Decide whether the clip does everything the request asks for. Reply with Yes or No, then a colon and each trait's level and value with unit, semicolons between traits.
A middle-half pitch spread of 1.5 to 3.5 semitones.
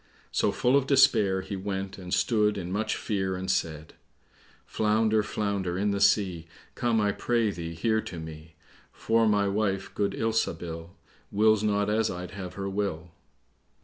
Yes: average, 3.0 semitones